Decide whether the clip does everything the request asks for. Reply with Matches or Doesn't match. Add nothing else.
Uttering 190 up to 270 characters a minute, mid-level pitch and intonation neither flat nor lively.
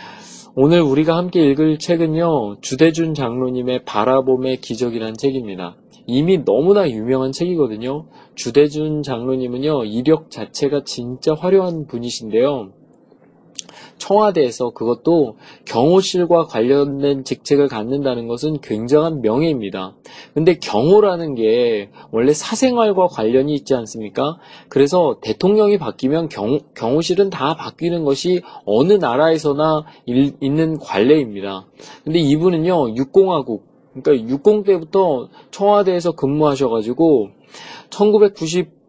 Doesn't match